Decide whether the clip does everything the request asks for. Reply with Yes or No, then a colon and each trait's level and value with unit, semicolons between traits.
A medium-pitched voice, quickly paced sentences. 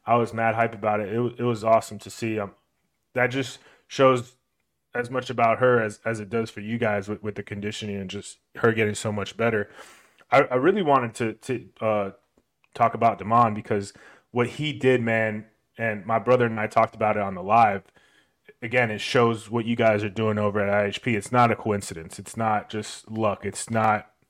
No: low, 110 Hz; fast, 215 wpm